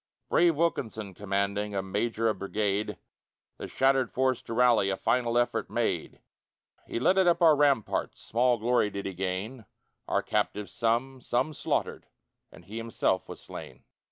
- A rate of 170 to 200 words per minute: No, average, 155 wpm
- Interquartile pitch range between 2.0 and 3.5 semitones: No, average, 4.2 semitones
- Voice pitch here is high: No, low, 115 Hz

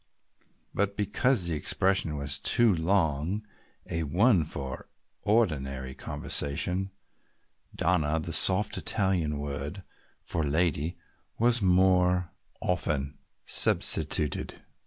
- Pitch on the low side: Yes, very low, 85 Hz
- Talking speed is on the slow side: Yes, slow, 95 wpm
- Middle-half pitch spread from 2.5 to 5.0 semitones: Yes, average, 4.7 semitones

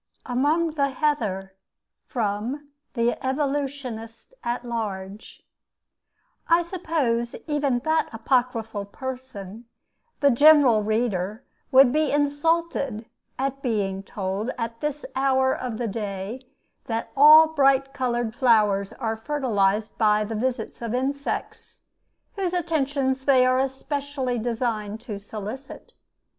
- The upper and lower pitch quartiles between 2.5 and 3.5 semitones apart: No, average, 4.2 semitones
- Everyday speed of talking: No, slow, 110 wpm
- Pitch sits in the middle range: No, very high, 250 Hz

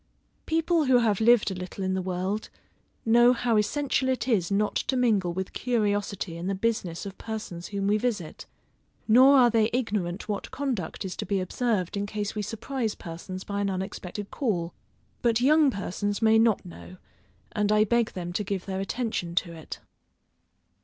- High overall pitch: Yes, high, 210 Hz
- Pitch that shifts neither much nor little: Yes, average, 4.0 semitones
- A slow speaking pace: No, average, 180 wpm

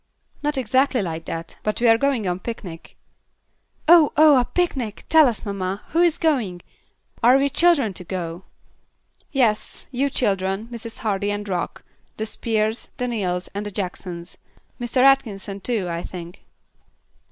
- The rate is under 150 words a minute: No, average, 155 wpm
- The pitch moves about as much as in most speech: No, wide, 5.7 semitones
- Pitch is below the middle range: No, high, 220 Hz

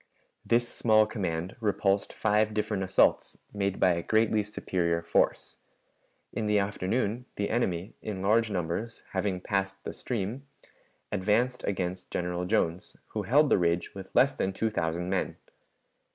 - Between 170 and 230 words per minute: No, average, 145 wpm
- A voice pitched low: Yes, low, 100 Hz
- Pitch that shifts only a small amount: No, average, 3.1 semitones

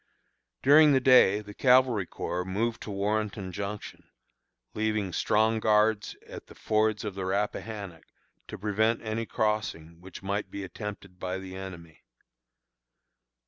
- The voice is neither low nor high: No, low, 105 Hz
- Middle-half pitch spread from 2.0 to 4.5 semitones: Yes, narrow, 2.4 semitones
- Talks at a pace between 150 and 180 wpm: No, slow, 135 wpm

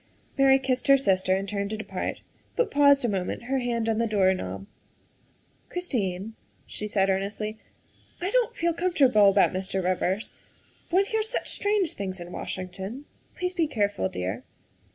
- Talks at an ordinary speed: Yes, average, 175 wpm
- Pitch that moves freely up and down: Yes, wide, 6.8 semitones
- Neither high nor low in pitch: No, high, 215 Hz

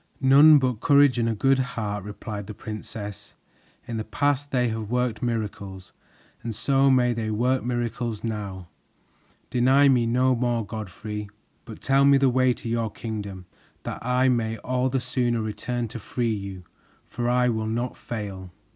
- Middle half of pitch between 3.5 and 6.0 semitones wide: No, average, 2.9 semitones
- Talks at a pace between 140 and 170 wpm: Yes, average, 165 wpm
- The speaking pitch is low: Yes, low, 120 Hz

